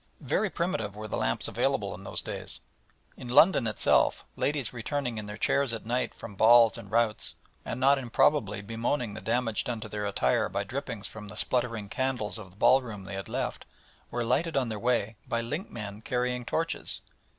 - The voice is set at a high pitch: No, low, 115 Hz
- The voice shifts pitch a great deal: No, average, 3.1 semitones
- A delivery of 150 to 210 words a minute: Yes, average, 185 wpm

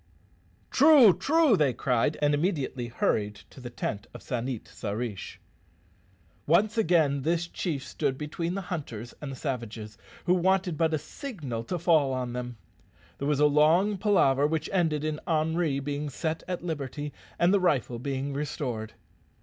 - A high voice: No, medium, 150 Hz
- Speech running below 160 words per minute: No, average, 165 wpm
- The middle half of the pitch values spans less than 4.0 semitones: No, average, 5.0 semitones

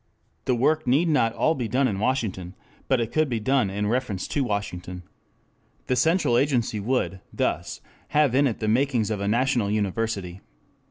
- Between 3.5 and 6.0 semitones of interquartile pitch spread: Yes, average, 4.5 semitones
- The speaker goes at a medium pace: Yes, average, 175 wpm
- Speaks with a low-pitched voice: Yes, low, 115 Hz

